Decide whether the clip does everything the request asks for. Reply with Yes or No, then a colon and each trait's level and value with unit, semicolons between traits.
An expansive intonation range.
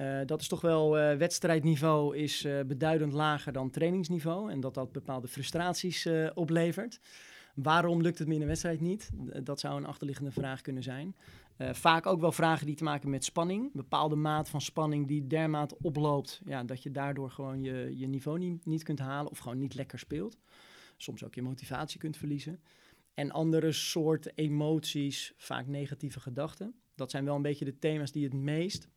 No: average, 2.7 semitones